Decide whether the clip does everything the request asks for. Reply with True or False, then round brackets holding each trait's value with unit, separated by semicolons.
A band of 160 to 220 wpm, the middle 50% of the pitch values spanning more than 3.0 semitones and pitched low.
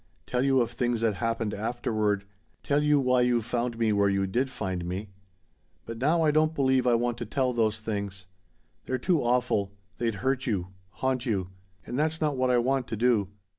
True (200 wpm; 3.6 semitones; 120 Hz)